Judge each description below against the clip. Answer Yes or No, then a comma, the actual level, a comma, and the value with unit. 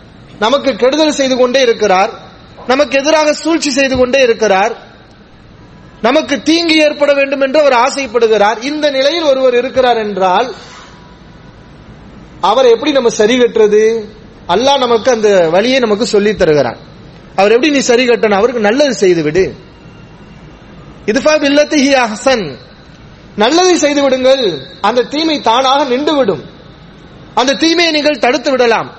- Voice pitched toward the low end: No, very high, 255 Hz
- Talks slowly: Yes, slow, 110 wpm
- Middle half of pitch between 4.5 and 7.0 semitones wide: Yes, average, 5.2 semitones